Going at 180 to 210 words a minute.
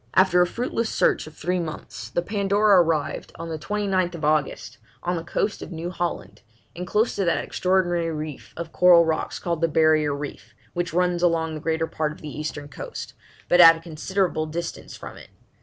Yes: average, 190 wpm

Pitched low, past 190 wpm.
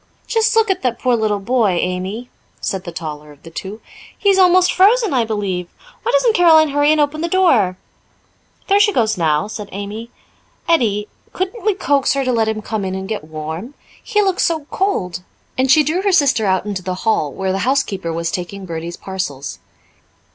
No: high, 220 Hz; average, 200 wpm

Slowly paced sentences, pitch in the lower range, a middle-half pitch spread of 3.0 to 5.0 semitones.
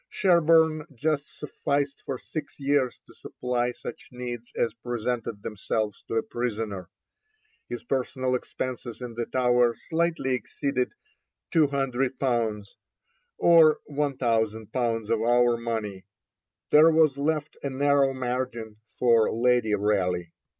Yes: slow, 115 wpm; low, 125 Hz; average, 3.7 semitones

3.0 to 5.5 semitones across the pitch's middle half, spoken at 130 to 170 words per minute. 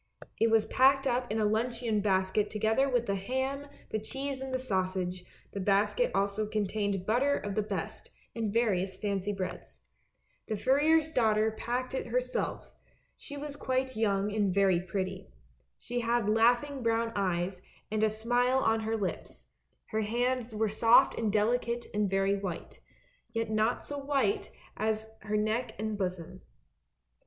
Yes: average, 3.5 semitones; average, 160 wpm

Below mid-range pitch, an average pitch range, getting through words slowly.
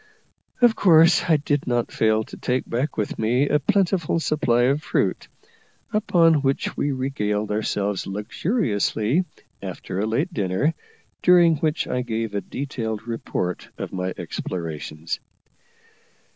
No: low, 125 Hz; wide, 6.8 semitones; slow, 130 wpm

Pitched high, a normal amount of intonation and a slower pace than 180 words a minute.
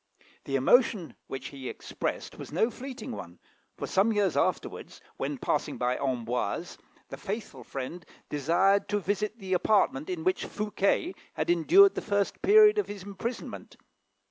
No: high, 195 Hz; wide, 7.1 semitones; average, 150 wpm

